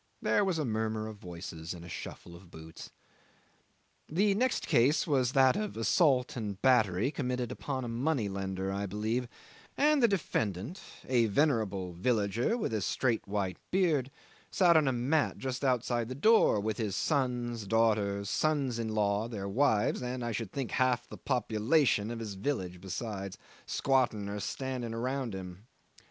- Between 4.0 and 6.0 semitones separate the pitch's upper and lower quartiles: Yes, average, 4.7 semitones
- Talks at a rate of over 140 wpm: Yes, average, 165 wpm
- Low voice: Yes, low, 115 Hz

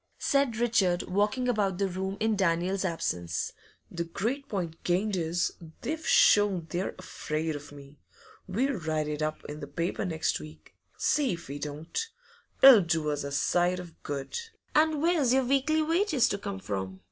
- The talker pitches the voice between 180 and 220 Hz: Yes, medium, 185 Hz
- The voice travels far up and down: Yes, wide, 7.2 semitones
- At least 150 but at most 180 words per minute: Yes, average, 170 wpm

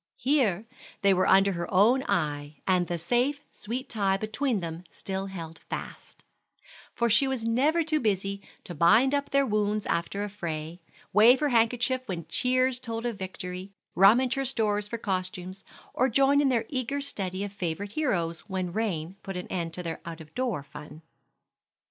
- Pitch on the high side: Yes, high, 205 Hz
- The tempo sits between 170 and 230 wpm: Yes, average, 175 wpm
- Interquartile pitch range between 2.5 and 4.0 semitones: No, wide, 5.6 semitones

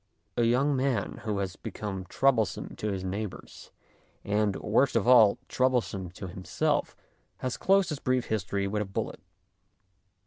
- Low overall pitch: Yes, low, 110 Hz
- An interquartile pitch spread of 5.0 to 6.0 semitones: No, average, 4.6 semitones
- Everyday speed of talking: Yes, average, 145 wpm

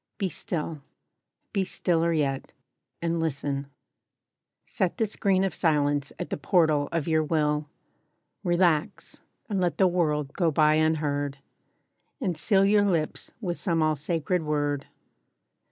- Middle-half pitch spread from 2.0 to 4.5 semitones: Yes, average, 3.3 semitones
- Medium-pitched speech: Yes, medium, 160 Hz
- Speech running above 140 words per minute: No, slow, 135 wpm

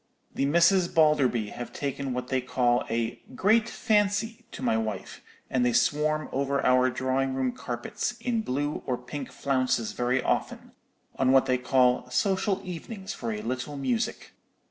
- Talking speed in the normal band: Yes, average, 160 wpm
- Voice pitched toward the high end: No, low, 130 Hz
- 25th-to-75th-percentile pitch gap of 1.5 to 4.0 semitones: No, average, 4.8 semitones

